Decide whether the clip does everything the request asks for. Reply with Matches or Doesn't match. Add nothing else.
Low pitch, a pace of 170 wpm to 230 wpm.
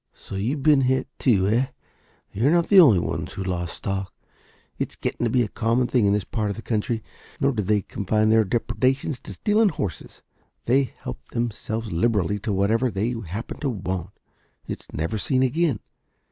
Matches